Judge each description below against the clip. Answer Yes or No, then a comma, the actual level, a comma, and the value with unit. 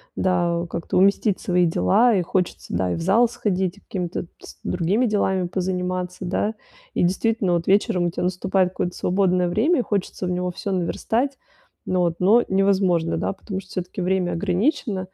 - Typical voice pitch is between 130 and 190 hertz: Yes, medium, 185 Hz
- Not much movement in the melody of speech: Yes, narrow, 2.1 semitones